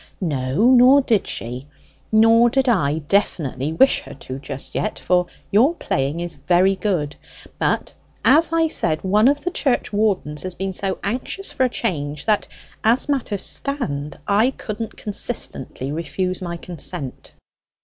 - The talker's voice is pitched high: Yes, high, 195 Hz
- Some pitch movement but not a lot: No, wide, 8.0 semitones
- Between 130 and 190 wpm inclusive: Yes, average, 150 wpm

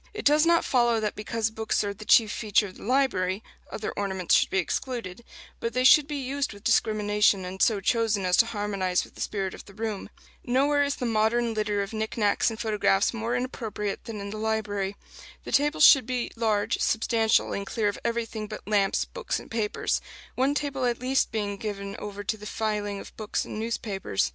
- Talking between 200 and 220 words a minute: Yes, fast, 205 wpm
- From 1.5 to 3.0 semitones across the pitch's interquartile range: Yes, narrow, 2.6 semitones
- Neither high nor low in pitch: No, high, 220 Hz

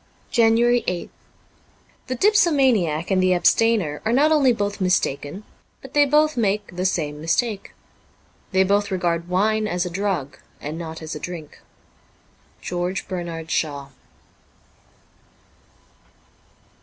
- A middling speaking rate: No, slow, 125 wpm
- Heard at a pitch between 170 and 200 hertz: Yes, high, 190 Hz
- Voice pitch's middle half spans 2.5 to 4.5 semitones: No, average, 5.3 semitones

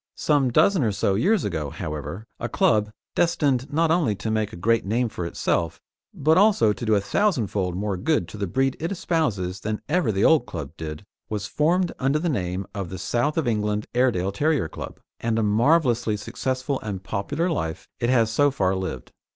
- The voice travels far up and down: Yes, wide, 6.9 semitones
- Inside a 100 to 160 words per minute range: No, average, 195 wpm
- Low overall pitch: Yes, low, 110 Hz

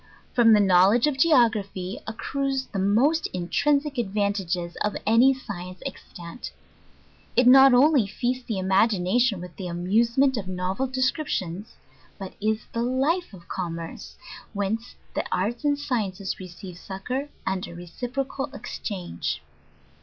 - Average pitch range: No, wide, 5.7 semitones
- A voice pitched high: Yes, high, 215 Hz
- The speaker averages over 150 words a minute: No, slow, 135 wpm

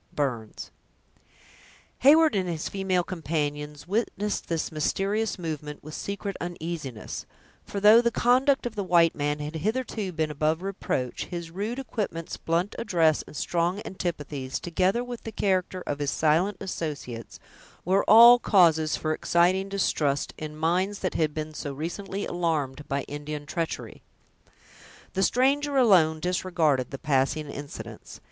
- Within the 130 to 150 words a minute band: Yes, average, 140 wpm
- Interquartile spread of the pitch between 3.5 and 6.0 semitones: Yes, average, 4.7 semitones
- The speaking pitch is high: No, medium, 170 Hz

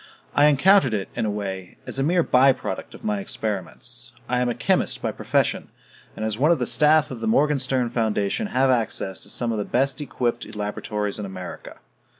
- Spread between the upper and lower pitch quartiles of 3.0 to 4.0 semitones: No, average, 4.6 semitones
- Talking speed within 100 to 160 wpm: No, average, 200 wpm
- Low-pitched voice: Yes, low, 120 Hz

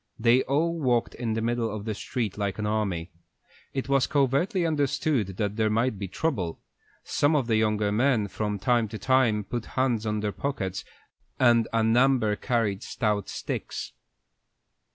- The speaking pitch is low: Yes, low, 115 Hz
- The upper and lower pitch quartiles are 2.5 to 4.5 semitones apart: Yes, average, 3.8 semitones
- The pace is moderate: Yes, average, 165 wpm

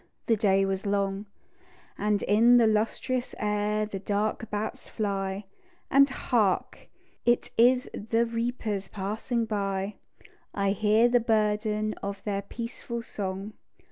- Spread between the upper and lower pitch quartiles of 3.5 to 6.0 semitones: No, narrow, 2.4 semitones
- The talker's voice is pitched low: No, high, 210 Hz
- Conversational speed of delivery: No, slow, 125 wpm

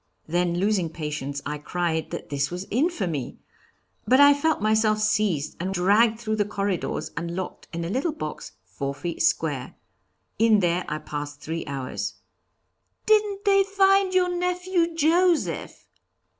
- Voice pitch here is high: Yes, high, 200 Hz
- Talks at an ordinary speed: Yes, average, 145 wpm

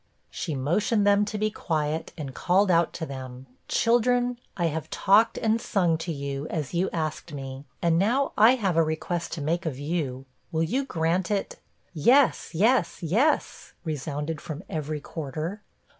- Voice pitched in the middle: Yes, medium, 165 Hz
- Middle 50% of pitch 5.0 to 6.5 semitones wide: Yes, average, 5.3 semitones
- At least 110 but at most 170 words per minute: Yes, average, 165 wpm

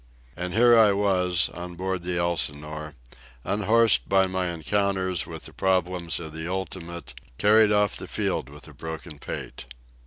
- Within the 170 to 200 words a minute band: No, average, 155 wpm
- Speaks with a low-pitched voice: Yes, very low, 90 Hz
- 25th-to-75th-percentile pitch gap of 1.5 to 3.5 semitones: Yes, average, 2.8 semitones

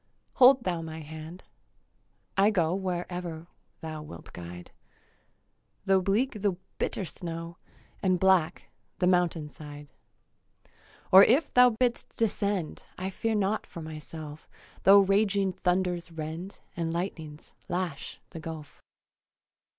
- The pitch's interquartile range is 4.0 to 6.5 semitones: No, average, 3.6 semitones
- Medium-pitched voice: Yes, medium, 180 Hz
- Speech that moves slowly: Yes, slow, 120 wpm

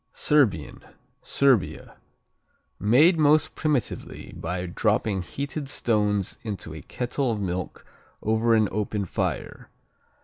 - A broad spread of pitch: Yes, wide, 6.0 semitones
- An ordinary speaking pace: No, slow, 105 wpm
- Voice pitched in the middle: No, low, 110 Hz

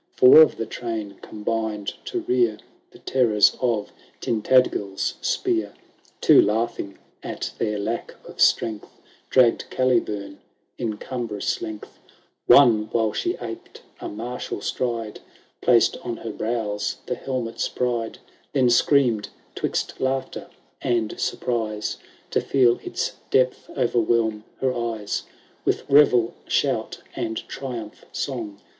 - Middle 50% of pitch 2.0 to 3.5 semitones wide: Yes, average, 2.9 semitones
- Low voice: Yes, low, 115 Hz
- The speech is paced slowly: Yes, slow, 120 wpm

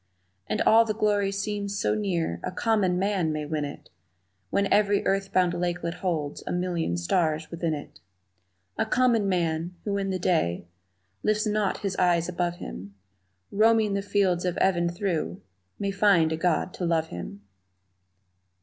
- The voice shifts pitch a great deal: No, average, 3.5 semitones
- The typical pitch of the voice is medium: Yes, medium, 180 Hz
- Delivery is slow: No, average, 160 wpm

